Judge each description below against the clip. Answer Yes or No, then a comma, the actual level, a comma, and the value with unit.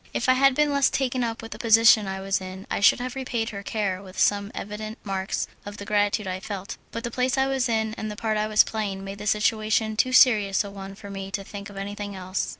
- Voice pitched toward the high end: Yes, high, 210 Hz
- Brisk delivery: Yes, fast, 255 wpm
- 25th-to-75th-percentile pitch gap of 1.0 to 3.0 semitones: Yes, narrow, 2.5 semitones